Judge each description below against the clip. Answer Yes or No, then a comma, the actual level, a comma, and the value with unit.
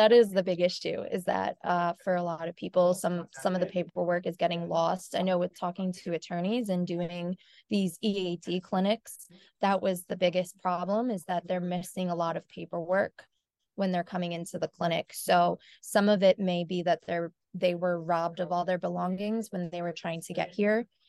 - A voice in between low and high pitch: Yes, medium, 180 Hz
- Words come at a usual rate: No, fast, 210 wpm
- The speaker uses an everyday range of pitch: No, narrow, 1.7 semitones